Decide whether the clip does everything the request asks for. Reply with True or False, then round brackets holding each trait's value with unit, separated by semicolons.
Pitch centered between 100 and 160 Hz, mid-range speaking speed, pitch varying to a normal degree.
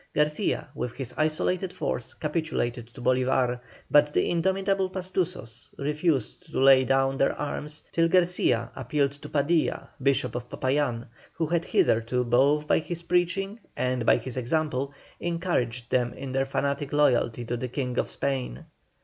True (140 Hz; 150 wpm; 4.6 semitones)